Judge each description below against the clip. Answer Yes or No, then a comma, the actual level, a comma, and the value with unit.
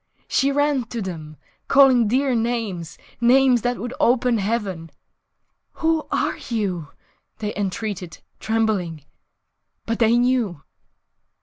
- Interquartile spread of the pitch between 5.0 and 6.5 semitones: No, average, 4.6 semitones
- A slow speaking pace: Yes, slow, 110 wpm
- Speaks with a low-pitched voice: No, high, 225 Hz